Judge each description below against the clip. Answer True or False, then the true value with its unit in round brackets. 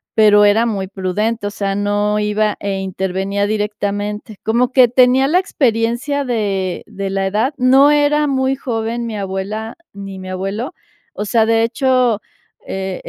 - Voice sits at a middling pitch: False (215 Hz)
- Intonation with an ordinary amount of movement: True (3.7 semitones)